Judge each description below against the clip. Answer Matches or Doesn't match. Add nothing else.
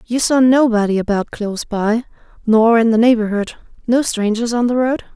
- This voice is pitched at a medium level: Doesn't match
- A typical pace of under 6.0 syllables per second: Matches